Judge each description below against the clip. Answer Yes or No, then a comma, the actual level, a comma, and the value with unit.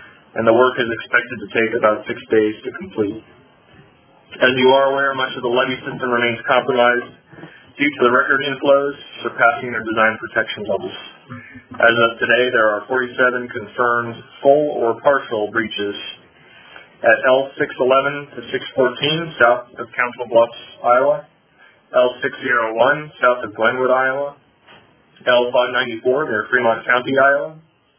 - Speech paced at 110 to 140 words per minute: Yes, slow, 135 wpm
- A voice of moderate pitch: No, low, 125 Hz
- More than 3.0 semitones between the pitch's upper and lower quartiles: No, average, 2.7 semitones